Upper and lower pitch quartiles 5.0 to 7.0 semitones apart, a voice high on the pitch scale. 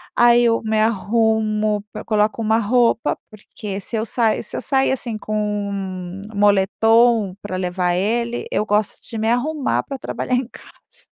No: narrow, 2.5 semitones; high, 220 Hz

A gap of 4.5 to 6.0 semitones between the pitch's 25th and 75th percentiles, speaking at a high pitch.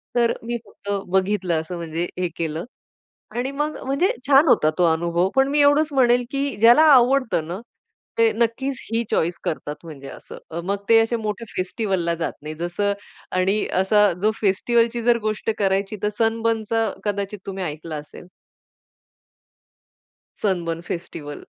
Yes: wide, 5.4 semitones; high, 210 Hz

